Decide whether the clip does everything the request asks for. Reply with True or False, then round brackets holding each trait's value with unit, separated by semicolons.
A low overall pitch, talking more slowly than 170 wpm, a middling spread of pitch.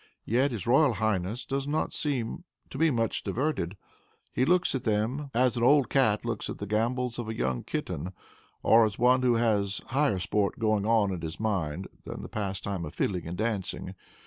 False (110 Hz; 195 wpm; 4.3 semitones)